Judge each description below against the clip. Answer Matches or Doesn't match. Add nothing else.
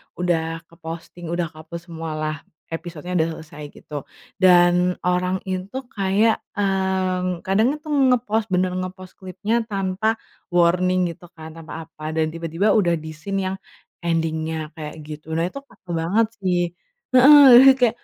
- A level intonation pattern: Doesn't match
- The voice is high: Doesn't match